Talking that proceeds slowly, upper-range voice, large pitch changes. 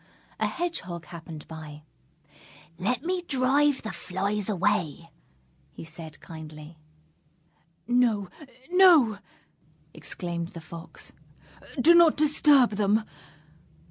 Yes: slow, 95 wpm; high, 205 Hz; wide, 8.5 semitones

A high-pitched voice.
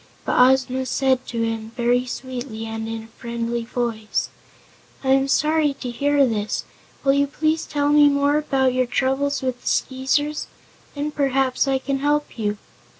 Yes: very high, 260 Hz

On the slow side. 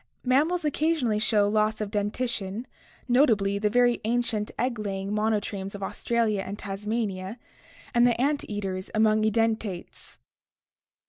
Yes: slow, 130 wpm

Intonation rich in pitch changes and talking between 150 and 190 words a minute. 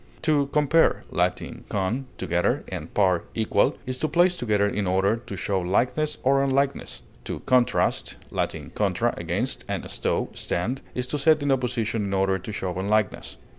Yes: wide, 5.9 semitones; average, 165 wpm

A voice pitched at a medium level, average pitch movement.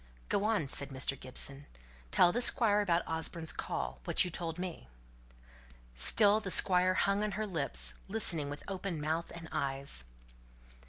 No: medium, 170 Hz; wide, 6.0 semitones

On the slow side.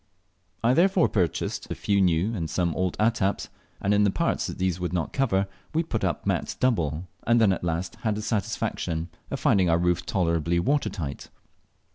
No: average, 185 wpm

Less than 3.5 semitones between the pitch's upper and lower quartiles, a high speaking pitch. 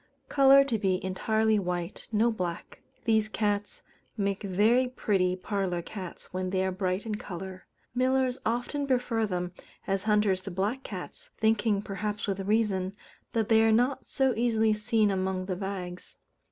Yes: average, 3.1 semitones; high, 210 Hz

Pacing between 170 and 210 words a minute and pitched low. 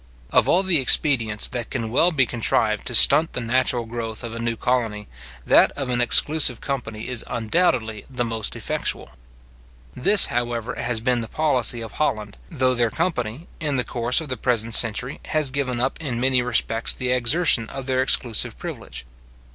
Yes: average, 180 wpm; low, 125 Hz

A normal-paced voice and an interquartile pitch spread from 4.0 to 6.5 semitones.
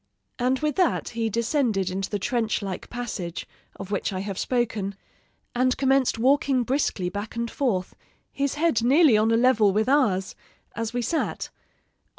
Yes: average, 160 wpm; average, 4.6 semitones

